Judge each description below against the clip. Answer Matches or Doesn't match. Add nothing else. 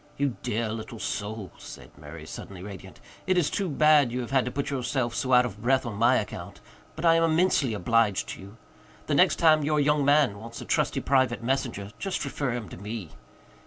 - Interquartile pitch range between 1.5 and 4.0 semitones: Doesn't match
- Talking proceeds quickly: Matches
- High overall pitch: Doesn't match